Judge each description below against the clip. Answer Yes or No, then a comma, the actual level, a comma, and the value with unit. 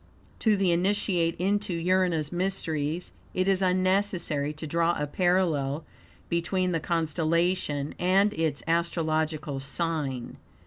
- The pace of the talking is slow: Yes, slow, 115 wpm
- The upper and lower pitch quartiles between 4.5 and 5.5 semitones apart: No, average, 3.0 semitones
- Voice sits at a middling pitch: Yes, medium, 170 Hz